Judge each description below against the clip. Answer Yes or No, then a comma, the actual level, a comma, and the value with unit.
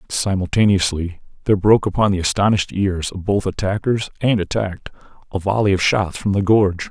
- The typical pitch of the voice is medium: No, very low, 95 Hz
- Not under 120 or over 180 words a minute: Yes, average, 165 wpm